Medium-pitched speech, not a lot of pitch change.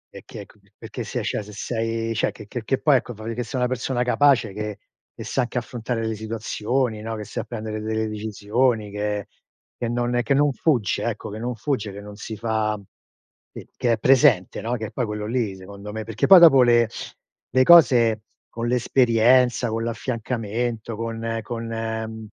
No: low, 115 Hz; narrow, 2.3 semitones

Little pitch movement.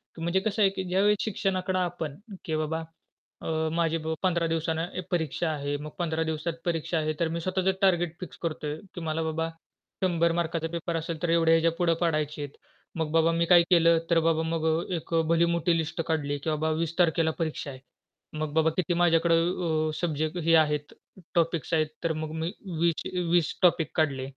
Yes: narrow, 1.5 semitones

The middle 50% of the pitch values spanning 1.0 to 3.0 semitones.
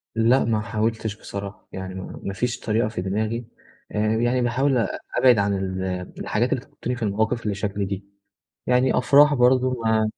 No: average, 3.6 semitones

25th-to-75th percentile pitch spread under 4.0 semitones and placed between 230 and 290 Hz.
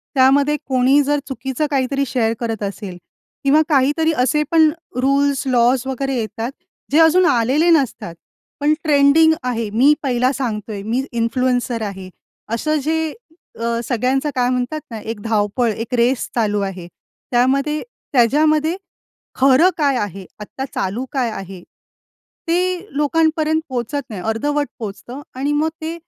No: average, 4.3 semitones; very high, 260 Hz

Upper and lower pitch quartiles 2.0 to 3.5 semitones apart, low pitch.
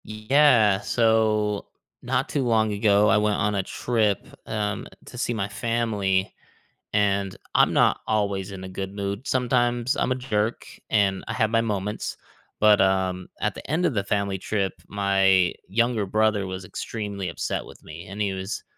Yes: narrow, 2.4 semitones; low, 105 Hz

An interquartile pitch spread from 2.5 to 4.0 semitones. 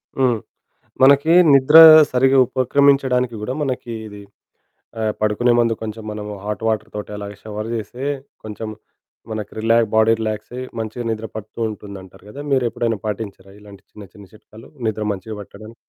Yes: average, 2.8 semitones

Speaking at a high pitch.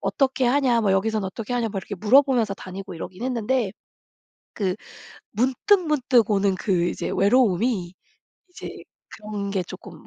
Yes: high, 215 Hz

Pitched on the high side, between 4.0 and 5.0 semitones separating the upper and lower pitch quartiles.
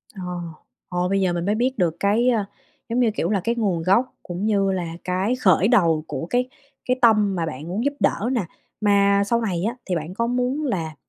Yes: high, 200 Hz; average, 4.7 semitones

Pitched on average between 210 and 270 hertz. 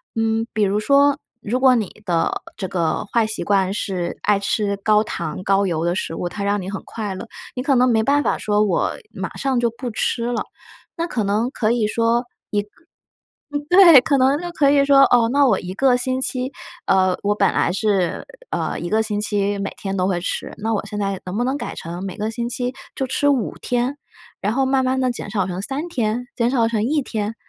Yes: high, 220 Hz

